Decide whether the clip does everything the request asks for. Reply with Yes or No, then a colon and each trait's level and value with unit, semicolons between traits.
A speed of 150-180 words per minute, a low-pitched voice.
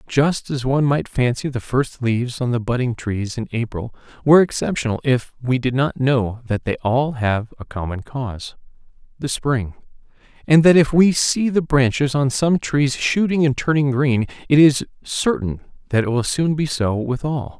No: average, 190 wpm; low, 130 Hz